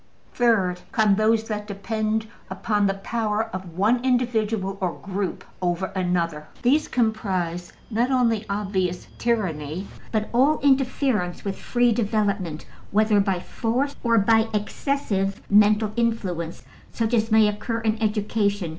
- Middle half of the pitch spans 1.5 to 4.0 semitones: Yes, average, 3.0 semitones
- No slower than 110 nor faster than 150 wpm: Yes, slow, 135 wpm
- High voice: Yes, high, 215 Hz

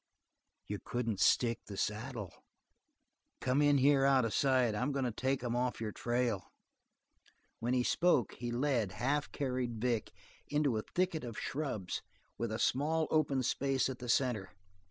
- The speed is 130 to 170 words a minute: Yes, average, 160 wpm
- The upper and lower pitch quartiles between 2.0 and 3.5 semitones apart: Yes, average, 3.0 semitones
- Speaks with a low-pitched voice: Yes, low, 125 Hz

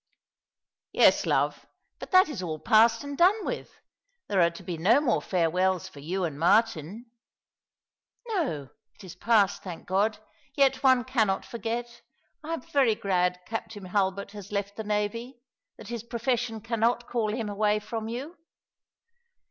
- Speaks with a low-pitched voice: No, high, 215 Hz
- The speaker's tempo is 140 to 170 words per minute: Yes, average, 165 wpm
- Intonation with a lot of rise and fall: No, average, 4.2 semitones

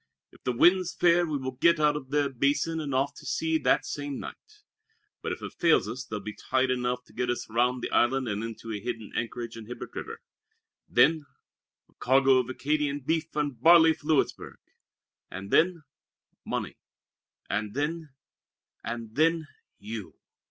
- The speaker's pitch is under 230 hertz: Yes, low, 135 Hz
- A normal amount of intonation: Yes, average, 4.6 semitones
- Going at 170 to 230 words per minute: Yes, average, 175 wpm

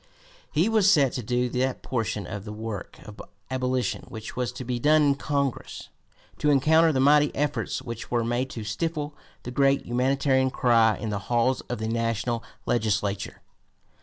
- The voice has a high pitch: No, low, 125 Hz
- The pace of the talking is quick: No, average, 170 wpm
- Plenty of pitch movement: No, average, 3.6 semitones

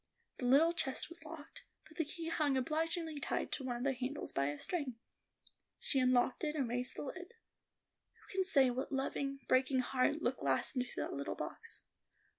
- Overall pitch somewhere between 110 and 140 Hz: No, very high, 275 Hz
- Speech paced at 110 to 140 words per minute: No, average, 190 wpm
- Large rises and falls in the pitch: No, average, 4.1 semitones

